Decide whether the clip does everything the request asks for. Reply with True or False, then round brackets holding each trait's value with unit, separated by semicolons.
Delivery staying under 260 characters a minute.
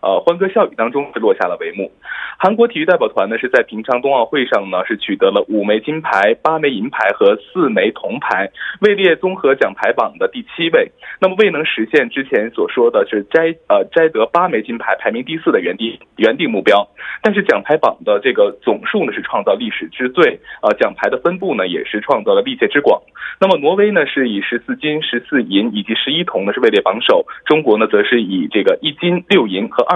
False (320 characters per minute)